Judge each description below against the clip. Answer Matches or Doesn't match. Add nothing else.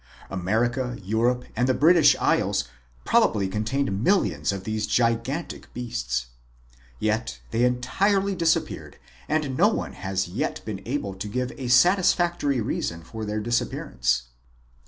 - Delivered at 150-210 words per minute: Doesn't match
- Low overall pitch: Matches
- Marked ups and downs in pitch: Matches